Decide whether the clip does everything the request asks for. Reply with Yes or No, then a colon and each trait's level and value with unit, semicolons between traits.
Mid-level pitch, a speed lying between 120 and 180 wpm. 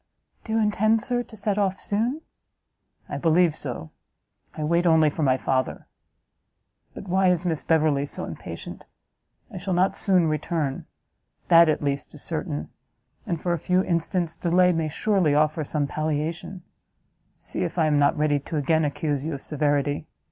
Yes: medium, 160 Hz; average, 170 wpm